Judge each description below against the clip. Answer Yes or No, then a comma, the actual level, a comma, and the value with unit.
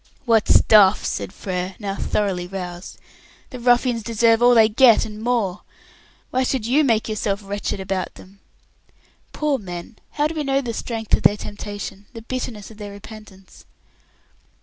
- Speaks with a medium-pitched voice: No, high, 215 Hz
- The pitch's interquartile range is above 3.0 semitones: Yes, average, 3.4 semitones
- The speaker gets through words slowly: No, average, 160 wpm